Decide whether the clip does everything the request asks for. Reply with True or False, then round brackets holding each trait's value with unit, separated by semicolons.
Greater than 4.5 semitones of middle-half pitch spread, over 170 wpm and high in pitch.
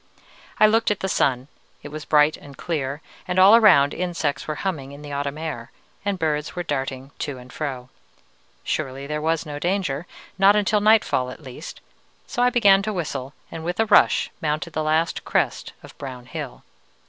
False (5.1 semitones; 185 wpm; 155 Hz)